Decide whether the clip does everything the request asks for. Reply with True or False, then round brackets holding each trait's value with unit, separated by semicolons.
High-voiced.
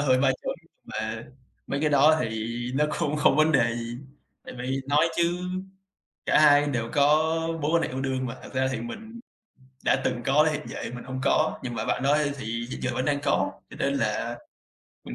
False (135 Hz)